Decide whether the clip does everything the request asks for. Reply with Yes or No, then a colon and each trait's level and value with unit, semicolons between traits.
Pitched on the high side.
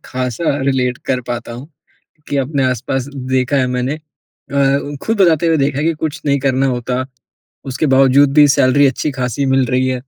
No: low, 135 Hz